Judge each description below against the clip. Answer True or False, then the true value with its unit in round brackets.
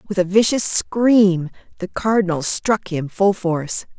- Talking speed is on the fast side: False (150 wpm)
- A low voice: False (190 Hz)